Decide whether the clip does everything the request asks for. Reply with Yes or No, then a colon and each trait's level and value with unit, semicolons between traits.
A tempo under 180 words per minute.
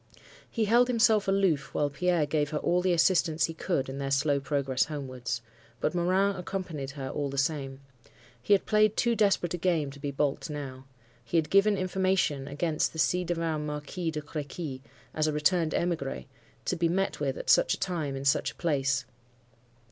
No: average, 190 wpm